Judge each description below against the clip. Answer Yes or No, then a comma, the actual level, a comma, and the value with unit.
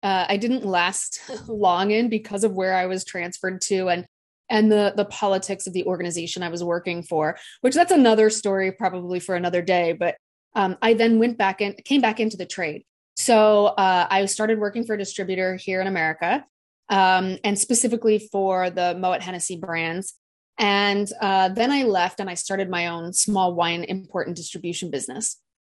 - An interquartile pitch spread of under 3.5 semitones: Yes, average, 2.7 semitones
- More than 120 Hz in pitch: Yes, high, 190 Hz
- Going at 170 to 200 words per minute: Yes, average, 185 wpm